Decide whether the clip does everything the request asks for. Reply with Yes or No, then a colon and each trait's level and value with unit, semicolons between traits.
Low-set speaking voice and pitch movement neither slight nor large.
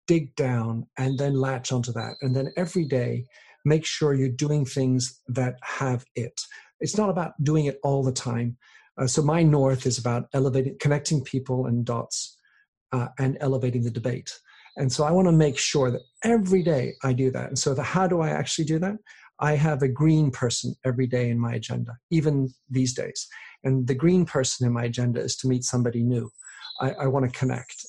Yes: low, 130 Hz; average, 3.0 semitones